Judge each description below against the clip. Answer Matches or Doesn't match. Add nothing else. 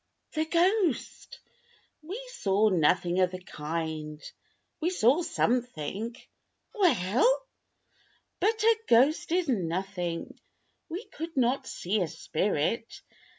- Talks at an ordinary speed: Doesn't match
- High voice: Matches